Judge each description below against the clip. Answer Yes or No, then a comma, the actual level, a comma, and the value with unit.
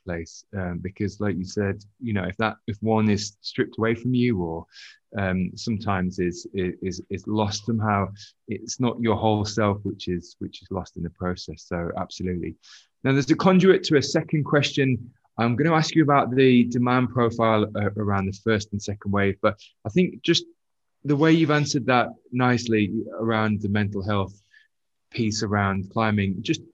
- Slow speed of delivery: No, average, 180 wpm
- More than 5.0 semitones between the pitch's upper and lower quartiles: No, average, 4.0 semitones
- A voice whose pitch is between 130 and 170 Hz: No, low, 110 Hz